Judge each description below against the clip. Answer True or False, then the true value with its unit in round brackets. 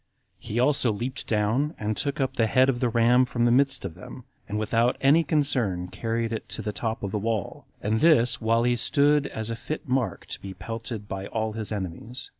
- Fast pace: True (220 wpm)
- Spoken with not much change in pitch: False (3.2 semitones)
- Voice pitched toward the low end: True (115 Hz)